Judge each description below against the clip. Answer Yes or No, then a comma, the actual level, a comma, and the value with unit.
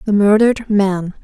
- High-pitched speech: Yes, high, 205 Hz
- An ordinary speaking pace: Yes, average, 145 wpm